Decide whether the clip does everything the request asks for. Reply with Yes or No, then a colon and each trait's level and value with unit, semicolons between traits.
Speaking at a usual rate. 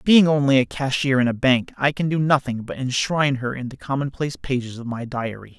No: fast, 225 wpm